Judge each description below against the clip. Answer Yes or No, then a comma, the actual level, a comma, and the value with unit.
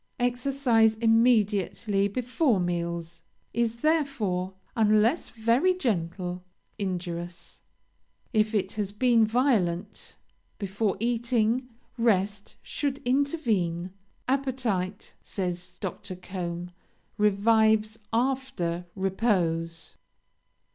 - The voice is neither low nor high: No, high, 215 Hz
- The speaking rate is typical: No, slow, 80 wpm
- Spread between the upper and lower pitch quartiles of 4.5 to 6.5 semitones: Yes, average, 4.8 semitones